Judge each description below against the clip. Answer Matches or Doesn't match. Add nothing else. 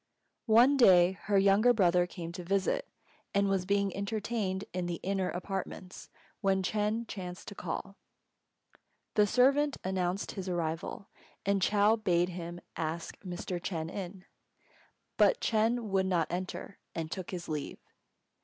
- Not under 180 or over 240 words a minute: Doesn't match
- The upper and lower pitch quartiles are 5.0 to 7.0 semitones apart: Doesn't match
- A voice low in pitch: Doesn't match